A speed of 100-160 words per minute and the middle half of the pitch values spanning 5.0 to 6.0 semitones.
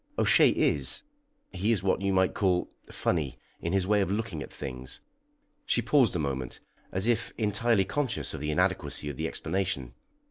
No: average, 175 wpm; wide, 5.4 semitones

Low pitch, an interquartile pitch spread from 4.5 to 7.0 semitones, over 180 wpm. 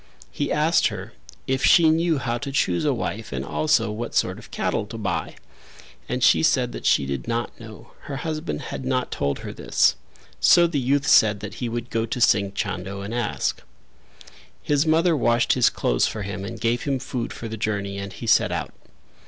Yes: low, 120 Hz; wide, 5.6 semitones; average, 200 wpm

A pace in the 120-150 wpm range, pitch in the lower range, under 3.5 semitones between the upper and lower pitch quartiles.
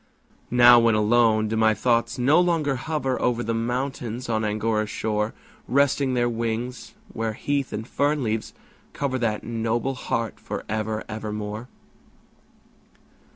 Yes: average, 140 wpm; low, 115 Hz; average, 2.7 semitones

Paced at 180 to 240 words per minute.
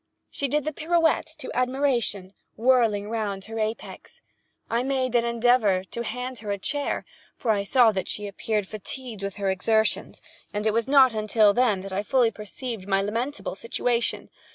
No: average, 170 wpm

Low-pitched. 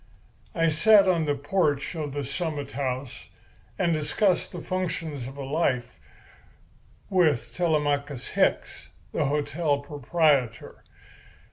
No: medium, 150 Hz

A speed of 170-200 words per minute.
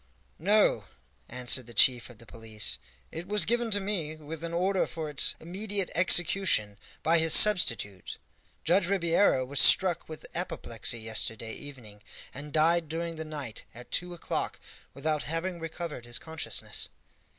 No: average, 150 wpm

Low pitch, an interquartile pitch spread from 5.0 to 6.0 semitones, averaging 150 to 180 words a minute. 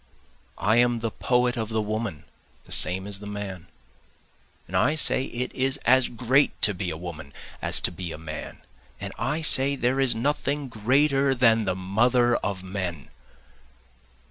Yes: low, 115 Hz; wide, 5.4 semitones; average, 170 wpm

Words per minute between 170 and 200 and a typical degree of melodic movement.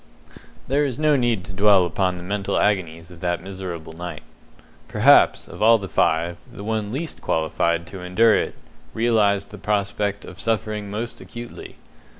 No: average, 160 wpm; average, 4.0 semitones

